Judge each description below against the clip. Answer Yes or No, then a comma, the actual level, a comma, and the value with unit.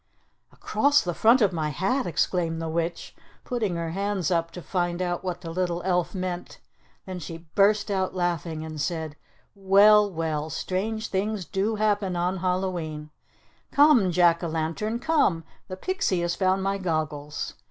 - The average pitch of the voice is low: No, medium, 180 Hz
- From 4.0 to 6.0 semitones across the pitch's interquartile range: No, average, 3.1 semitones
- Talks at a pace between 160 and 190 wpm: Yes, average, 165 wpm